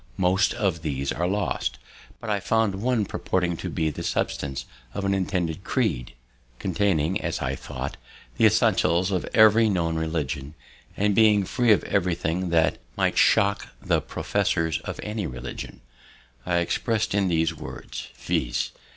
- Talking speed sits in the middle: Yes, average, 150 wpm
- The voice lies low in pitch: Yes, very low, 90 Hz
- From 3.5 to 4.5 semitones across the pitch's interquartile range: Yes, average, 4.1 semitones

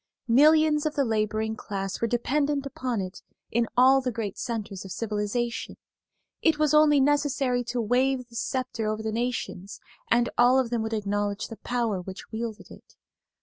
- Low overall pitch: No, high, 235 Hz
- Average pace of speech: Yes, average, 170 wpm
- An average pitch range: Yes, average, 3.6 semitones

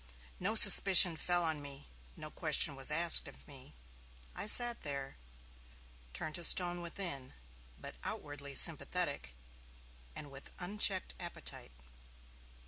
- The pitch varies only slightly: No, average, 4.5 semitones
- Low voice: No, medium, 160 Hz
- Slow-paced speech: Yes, slow, 120 wpm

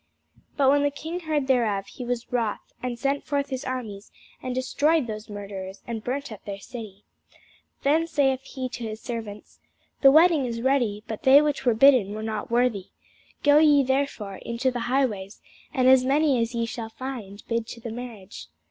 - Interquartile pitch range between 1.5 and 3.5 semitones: No, average, 3.9 semitones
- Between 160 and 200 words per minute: Yes, average, 190 wpm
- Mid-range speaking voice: No, high, 245 Hz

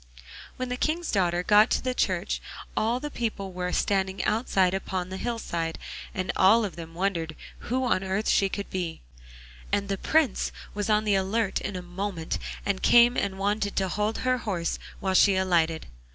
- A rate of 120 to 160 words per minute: No, average, 180 wpm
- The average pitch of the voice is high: Yes, high, 195 Hz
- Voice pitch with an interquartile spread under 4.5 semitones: Yes, average, 2.9 semitones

